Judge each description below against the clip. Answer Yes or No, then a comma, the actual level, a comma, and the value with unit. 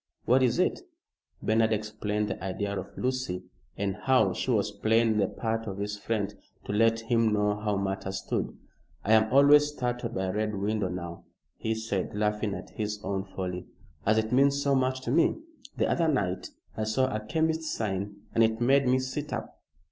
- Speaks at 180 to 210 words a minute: Yes, average, 190 wpm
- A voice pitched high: No, low, 110 Hz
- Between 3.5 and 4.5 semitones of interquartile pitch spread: Yes, average, 3.8 semitones